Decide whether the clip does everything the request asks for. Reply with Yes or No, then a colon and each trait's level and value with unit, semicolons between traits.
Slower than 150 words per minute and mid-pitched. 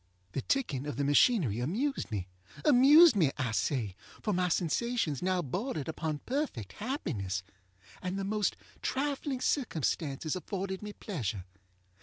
Yes: slow, 135 wpm; medium, 180 Hz